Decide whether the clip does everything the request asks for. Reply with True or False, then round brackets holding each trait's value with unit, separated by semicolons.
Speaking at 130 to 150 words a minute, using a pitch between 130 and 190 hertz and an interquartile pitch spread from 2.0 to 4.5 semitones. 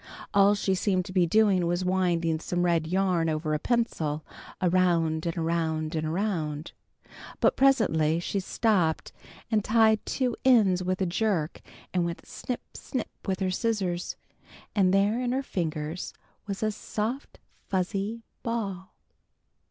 True (145 wpm; 185 Hz; 4.2 semitones)